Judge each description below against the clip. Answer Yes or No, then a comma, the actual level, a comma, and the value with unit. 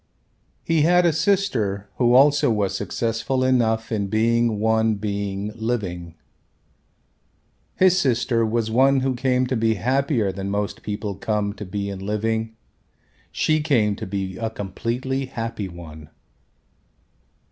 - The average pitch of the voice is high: No, low, 110 Hz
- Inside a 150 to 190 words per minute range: No, slow, 135 wpm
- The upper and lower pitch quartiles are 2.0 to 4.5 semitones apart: Yes, average, 4.1 semitones